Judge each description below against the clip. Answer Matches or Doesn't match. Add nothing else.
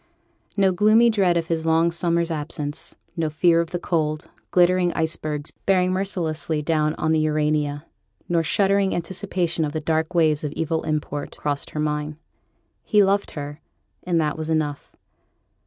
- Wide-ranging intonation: Doesn't match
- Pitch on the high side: Doesn't match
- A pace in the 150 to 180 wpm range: Matches